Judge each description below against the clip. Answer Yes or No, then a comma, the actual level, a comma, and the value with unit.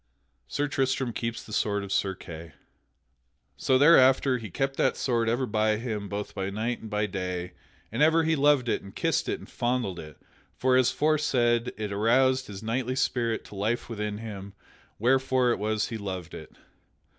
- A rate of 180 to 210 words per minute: Yes, average, 185 wpm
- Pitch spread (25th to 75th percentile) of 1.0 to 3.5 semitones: No, average, 4.2 semitones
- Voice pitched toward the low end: Yes, low, 115 Hz